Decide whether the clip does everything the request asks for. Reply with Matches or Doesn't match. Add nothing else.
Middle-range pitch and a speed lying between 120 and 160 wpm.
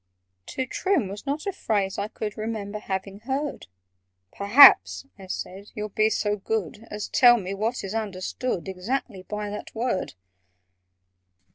Doesn't match